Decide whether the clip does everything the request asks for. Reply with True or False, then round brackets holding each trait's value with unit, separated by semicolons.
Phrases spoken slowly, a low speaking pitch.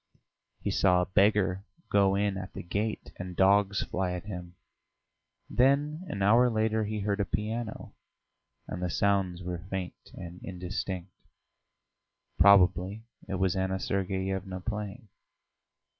True (130 wpm; 95 Hz)